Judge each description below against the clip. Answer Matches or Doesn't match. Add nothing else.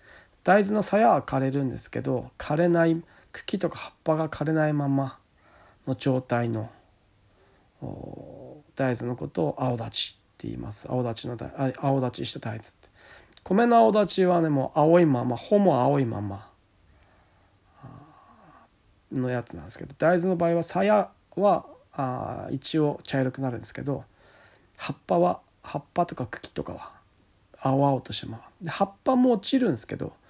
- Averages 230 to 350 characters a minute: Matches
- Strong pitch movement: Matches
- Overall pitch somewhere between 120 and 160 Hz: Matches